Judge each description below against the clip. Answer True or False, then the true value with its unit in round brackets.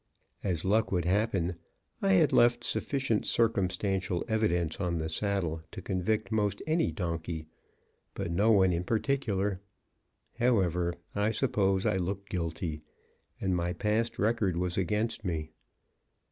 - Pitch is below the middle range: True (95 Hz)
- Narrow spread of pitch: False (3.8 semitones)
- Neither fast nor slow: False (130 wpm)